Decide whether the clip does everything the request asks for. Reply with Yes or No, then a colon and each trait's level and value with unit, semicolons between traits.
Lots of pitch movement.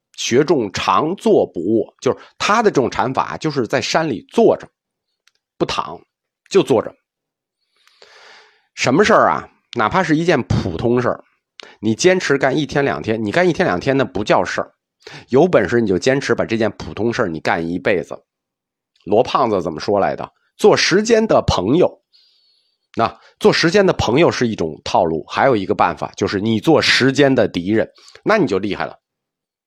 Yes: wide, 8.9 semitones